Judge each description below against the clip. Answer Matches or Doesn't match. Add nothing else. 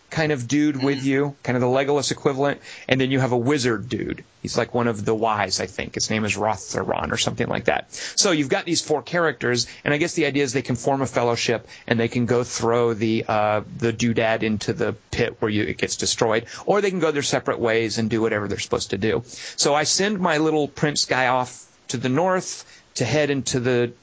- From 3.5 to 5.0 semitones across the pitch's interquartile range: Matches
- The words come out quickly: Matches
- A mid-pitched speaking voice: Doesn't match